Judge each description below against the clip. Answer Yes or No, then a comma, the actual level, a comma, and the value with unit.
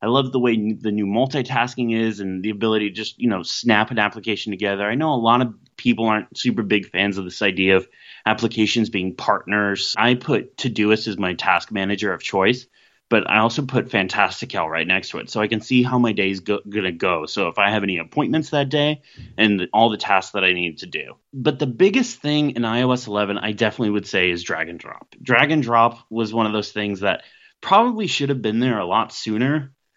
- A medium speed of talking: No, fast, 225 wpm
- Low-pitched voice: Yes, low, 110 Hz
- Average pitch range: Yes, average, 3.3 semitones